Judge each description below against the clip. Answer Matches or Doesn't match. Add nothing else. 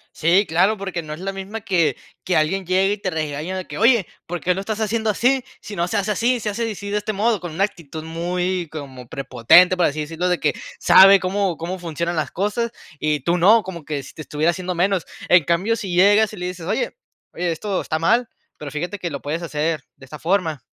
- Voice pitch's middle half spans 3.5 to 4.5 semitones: Matches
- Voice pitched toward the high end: Doesn't match